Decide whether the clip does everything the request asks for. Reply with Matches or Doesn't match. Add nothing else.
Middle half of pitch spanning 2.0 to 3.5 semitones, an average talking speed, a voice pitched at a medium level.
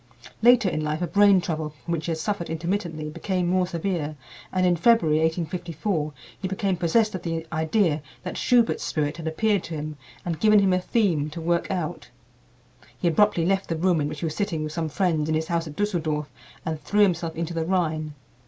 Doesn't match